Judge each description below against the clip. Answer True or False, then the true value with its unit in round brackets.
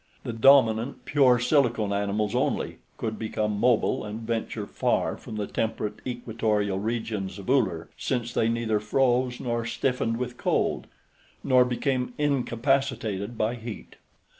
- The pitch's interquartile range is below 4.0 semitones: True (2.7 semitones)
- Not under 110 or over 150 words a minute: True (135 wpm)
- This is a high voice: False (115 Hz)